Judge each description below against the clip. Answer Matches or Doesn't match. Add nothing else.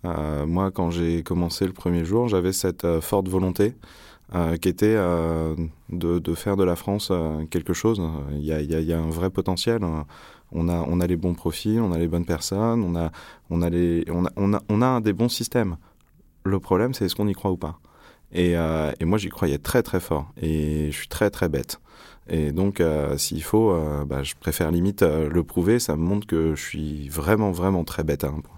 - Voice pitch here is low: Matches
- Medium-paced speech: Doesn't match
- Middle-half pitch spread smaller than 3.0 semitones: Doesn't match